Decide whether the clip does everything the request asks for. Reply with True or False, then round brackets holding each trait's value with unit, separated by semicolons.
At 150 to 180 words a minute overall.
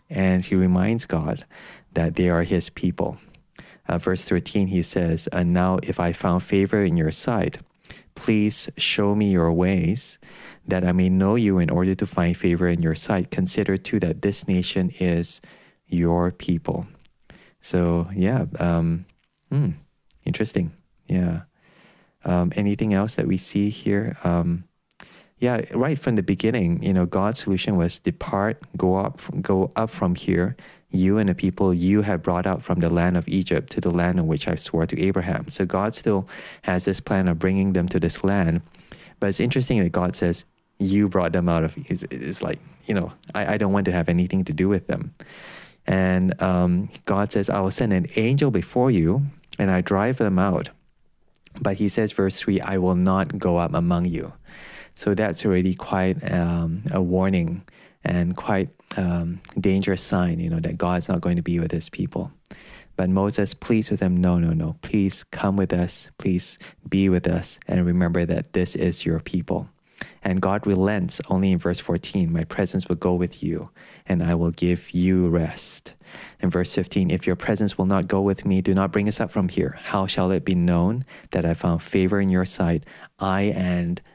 False (190 wpm)